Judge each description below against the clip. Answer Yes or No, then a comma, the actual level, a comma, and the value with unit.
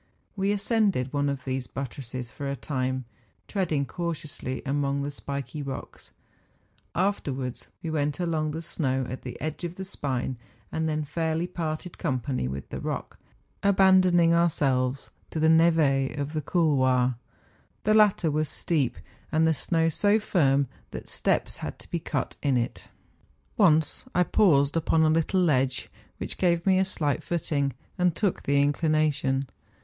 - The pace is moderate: Yes, average, 160 wpm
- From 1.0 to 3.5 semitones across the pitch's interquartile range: No, average, 3.9 semitones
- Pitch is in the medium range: Yes, medium, 155 Hz